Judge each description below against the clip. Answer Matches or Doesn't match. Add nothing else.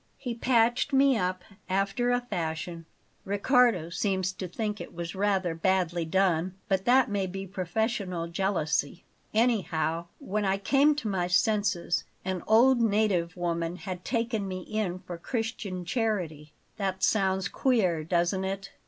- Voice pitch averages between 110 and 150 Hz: Doesn't match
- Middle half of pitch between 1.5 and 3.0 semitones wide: Doesn't match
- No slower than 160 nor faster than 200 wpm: Doesn't match